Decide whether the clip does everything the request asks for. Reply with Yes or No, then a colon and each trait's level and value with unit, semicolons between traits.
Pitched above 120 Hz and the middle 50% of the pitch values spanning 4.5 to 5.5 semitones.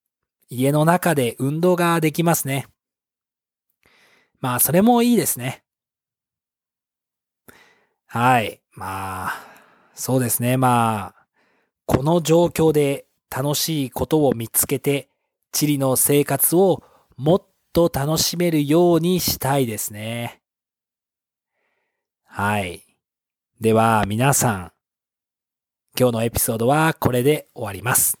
Yes: low, 135 Hz; average, 5.2 semitones